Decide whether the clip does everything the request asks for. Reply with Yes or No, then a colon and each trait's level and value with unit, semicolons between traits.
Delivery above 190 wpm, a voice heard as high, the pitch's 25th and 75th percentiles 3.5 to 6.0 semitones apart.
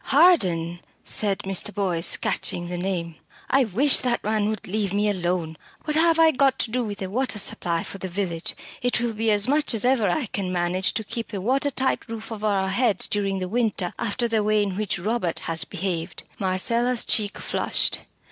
Yes: average, 200 wpm; high, 205 Hz; average, 4.4 semitones